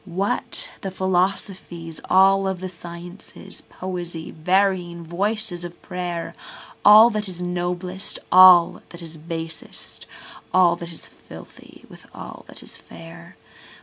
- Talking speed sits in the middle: No, slow, 115 wpm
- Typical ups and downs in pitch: No, narrow, 1.8 semitones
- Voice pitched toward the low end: No, medium, 180 Hz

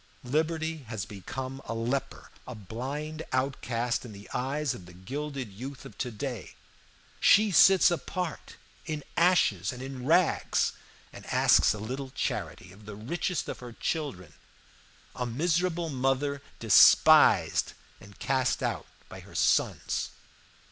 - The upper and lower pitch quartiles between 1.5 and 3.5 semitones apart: No, average, 5.0 semitones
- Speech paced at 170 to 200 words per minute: No, slow, 135 wpm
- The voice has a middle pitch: No, low, 130 Hz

